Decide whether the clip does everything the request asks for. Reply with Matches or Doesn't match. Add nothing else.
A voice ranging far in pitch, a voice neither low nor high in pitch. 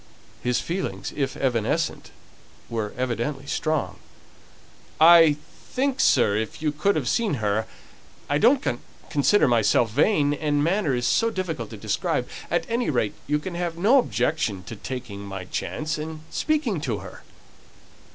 Matches